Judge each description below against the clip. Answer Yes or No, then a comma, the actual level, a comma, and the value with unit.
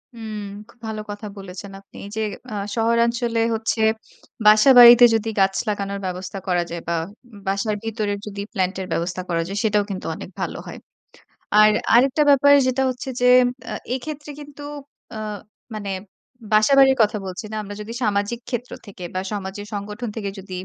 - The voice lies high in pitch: Yes, high, 215 Hz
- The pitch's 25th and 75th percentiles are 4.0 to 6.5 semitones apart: No, average, 3.2 semitones